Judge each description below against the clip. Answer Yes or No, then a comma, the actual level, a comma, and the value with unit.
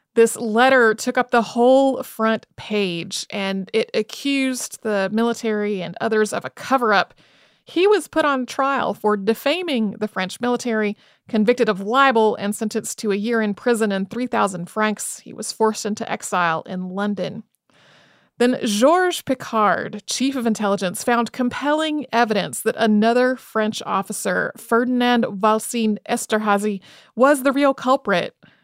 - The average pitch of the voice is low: No, high, 225 Hz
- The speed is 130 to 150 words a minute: Yes, average, 145 wpm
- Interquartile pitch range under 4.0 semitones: Yes, average, 3.2 semitones